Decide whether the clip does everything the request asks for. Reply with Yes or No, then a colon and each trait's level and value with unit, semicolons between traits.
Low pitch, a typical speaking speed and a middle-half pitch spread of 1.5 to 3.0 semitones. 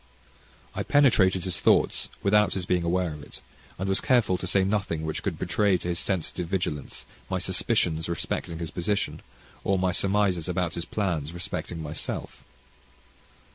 Yes: very low, 90 Hz; average, 160 wpm; narrow, 2.6 semitones